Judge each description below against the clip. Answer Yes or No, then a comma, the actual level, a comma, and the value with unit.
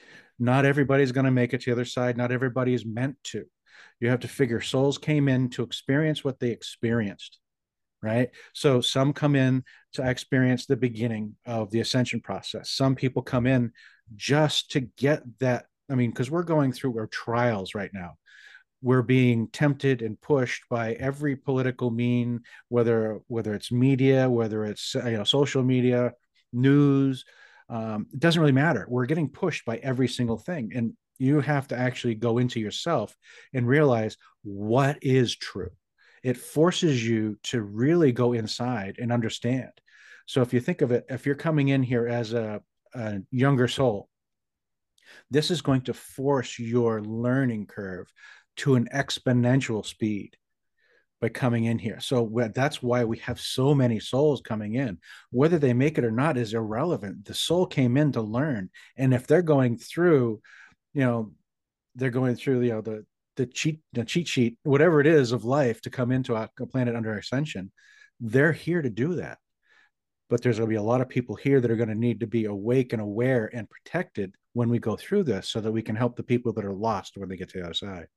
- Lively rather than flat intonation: No, average, 2.9 semitones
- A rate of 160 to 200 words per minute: Yes, average, 190 wpm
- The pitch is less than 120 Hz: No, low, 125 Hz